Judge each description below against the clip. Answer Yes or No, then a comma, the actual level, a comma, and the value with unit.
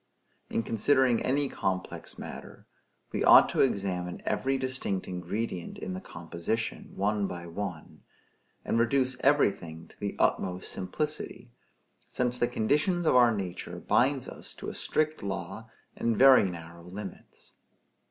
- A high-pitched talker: No, low, 105 Hz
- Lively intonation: Yes, wide, 6.1 semitones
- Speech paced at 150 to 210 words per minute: No, slow, 135 wpm